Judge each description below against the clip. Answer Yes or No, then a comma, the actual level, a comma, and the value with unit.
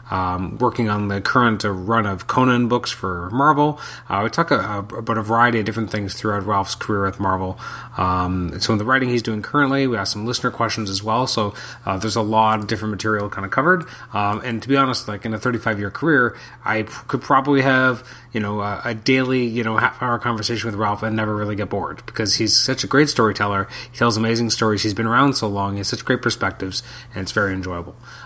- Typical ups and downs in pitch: Yes, average, 3.1 semitones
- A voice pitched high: No, low, 110 Hz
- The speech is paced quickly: Yes, fast, 235 wpm